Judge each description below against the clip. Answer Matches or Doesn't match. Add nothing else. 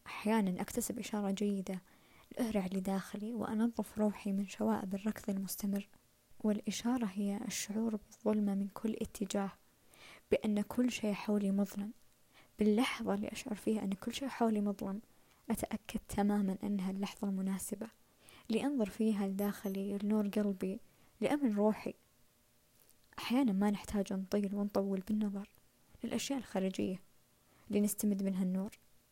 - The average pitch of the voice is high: Matches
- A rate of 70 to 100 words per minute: Doesn't match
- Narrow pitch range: Matches